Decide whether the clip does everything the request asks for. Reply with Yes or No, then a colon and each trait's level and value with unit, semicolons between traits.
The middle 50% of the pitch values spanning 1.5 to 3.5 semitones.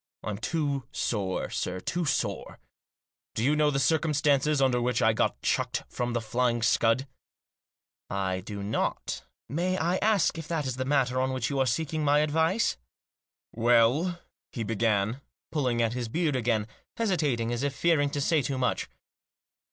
No: average, 4.7 semitones